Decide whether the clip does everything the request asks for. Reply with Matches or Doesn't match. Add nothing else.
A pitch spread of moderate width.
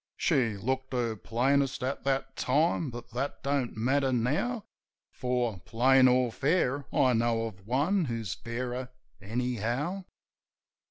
Matches